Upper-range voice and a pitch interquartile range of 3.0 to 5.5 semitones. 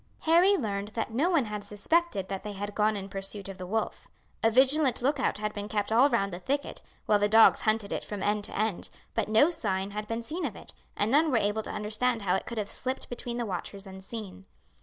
Yes: high, 215 Hz; average, 3.7 semitones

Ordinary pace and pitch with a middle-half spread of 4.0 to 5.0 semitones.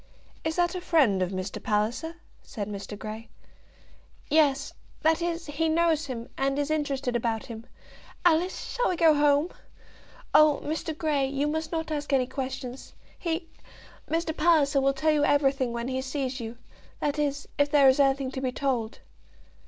No: average, 170 wpm; average, 3.6 semitones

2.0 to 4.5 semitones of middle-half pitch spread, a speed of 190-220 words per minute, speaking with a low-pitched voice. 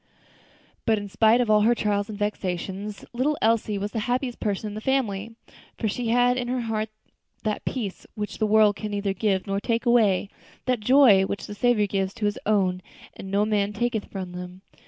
No: narrow, 2.5 semitones; average, 200 wpm; high, 210 Hz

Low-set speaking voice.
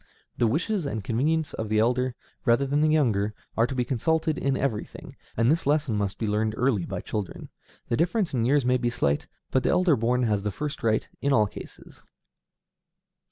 Yes: low, 125 Hz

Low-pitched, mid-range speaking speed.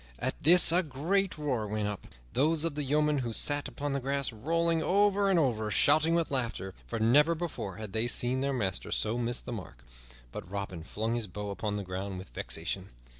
No: low, 125 Hz; fast, 210 wpm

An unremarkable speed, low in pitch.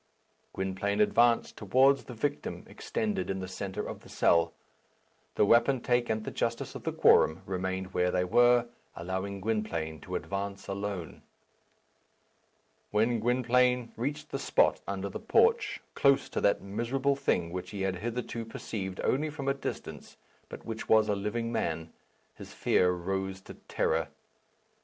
Yes: average, 150 wpm; low, 105 Hz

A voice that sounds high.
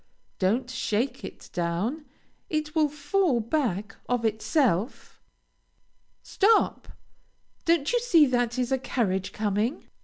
Yes: very high, 250 Hz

